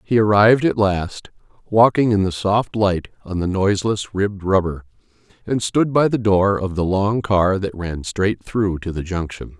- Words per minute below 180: No, average, 190 wpm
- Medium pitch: No, low, 100 Hz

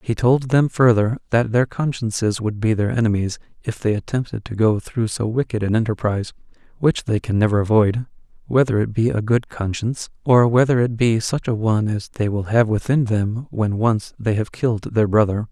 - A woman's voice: No, male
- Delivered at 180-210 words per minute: Yes, average, 200 wpm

